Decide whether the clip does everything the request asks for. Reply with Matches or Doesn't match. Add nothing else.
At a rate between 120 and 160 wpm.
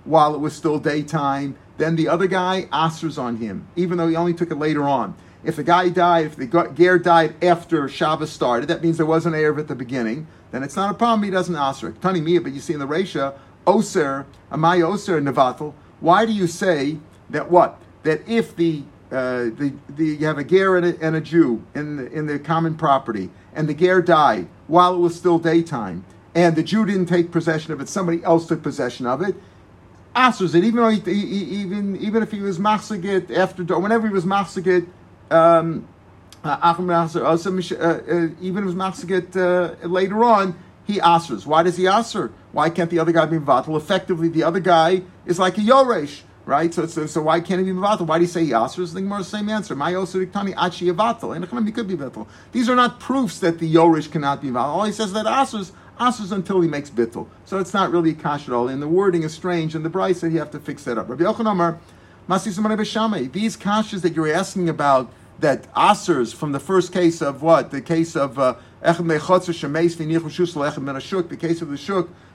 Doesn't match